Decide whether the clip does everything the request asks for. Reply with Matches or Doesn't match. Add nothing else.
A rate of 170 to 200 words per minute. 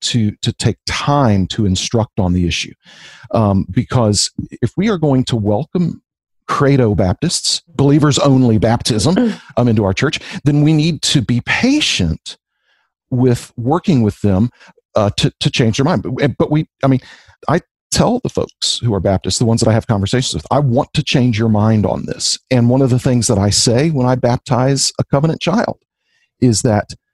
Matches